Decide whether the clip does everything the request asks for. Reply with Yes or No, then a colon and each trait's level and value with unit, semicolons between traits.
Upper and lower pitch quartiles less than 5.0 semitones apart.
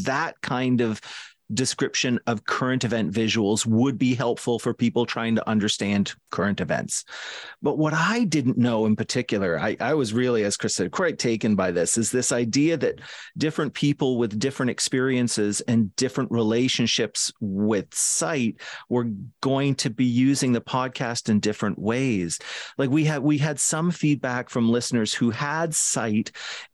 Yes: average, 3.2 semitones